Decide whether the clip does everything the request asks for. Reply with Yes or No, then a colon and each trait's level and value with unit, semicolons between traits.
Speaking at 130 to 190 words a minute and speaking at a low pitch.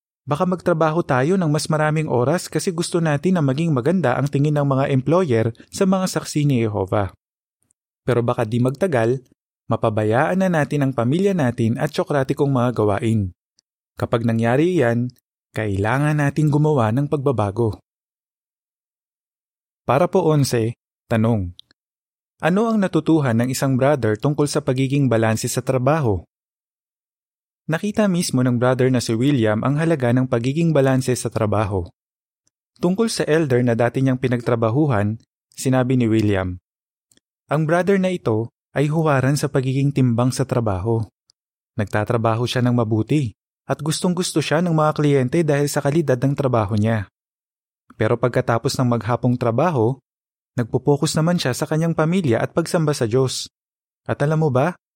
Yes: average, 145 wpm; low, 130 Hz